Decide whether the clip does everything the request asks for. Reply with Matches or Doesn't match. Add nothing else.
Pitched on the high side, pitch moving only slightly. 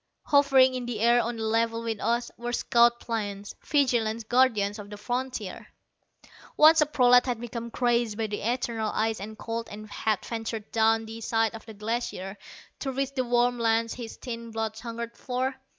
Matches